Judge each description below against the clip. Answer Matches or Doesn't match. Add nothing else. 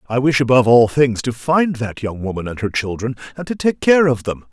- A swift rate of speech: Matches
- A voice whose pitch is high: Doesn't match